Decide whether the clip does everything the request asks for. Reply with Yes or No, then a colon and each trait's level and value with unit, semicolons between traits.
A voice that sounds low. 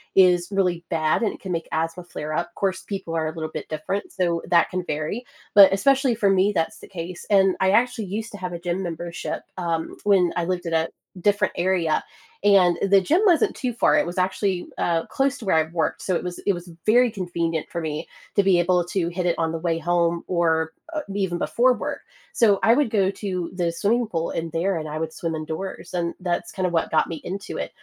No: medium, 180 Hz